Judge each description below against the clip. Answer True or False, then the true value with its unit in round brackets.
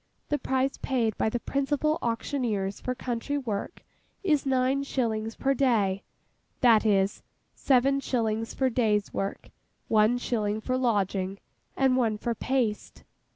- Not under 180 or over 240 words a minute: False (135 wpm)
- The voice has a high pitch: True (240 Hz)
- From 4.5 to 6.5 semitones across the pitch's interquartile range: False (3.7 semitones)